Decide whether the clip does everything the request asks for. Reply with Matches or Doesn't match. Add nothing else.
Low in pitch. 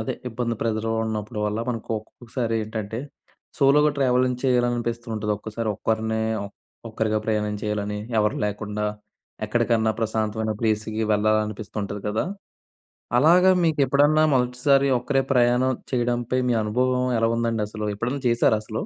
Matches